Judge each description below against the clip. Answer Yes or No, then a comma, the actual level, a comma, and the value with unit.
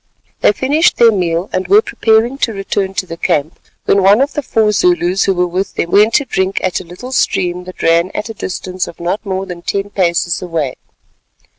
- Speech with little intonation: No, average, 3.6 semitones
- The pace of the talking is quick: Yes, fast, 210 wpm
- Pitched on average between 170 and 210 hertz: Yes, high, 190 Hz